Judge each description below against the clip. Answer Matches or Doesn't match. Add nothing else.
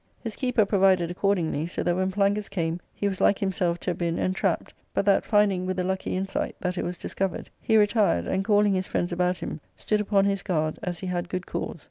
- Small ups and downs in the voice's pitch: Matches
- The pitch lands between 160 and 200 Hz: Matches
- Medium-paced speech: Doesn't match